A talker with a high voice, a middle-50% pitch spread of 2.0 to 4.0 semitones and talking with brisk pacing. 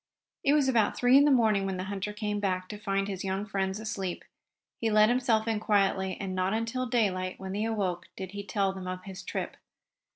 Yes: high, 200 Hz; narrow, 2.5 semitones; fast, 220 wpm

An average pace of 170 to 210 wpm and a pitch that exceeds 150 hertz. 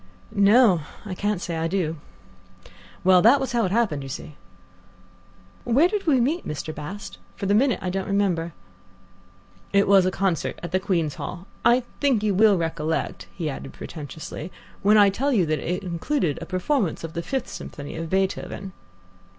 Yes: average, 175 wpm; high, 190 Hz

